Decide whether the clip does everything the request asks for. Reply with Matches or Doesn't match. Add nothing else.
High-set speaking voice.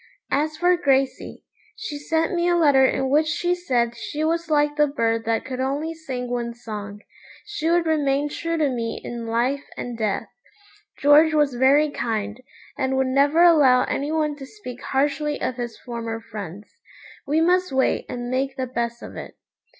Matches